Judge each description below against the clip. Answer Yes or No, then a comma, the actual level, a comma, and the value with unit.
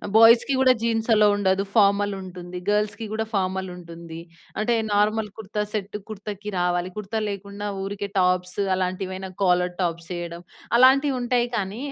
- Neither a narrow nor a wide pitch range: Yes, average, 3.0 semitones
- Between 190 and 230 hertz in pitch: Yes, high, 200 Hz